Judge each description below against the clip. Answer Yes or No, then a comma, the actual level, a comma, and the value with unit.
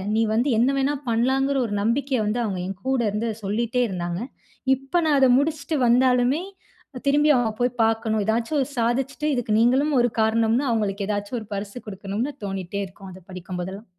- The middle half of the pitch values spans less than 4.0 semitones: No, average, 4.4 semitones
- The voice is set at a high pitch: Yes, high, 230 Hz